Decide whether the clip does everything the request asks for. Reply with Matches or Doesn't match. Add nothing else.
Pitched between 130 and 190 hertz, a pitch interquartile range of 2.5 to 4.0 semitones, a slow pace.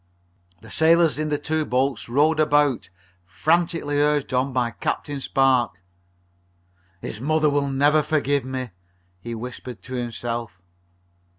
Matches